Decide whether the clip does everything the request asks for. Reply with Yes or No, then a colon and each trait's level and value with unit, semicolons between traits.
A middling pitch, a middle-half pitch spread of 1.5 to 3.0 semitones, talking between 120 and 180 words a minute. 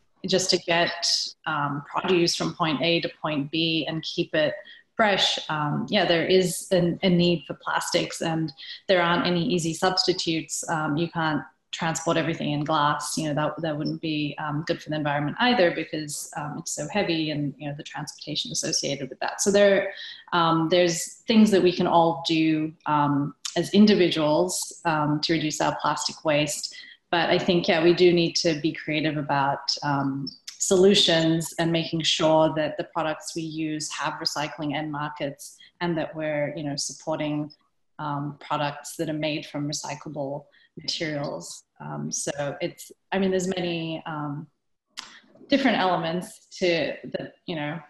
Yes: medium, 165 Hz; average, 2.7 semitones; average, 170 wpm